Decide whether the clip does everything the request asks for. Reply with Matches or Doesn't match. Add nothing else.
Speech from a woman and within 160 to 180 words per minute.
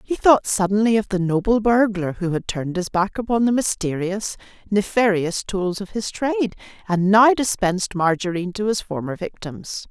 Matches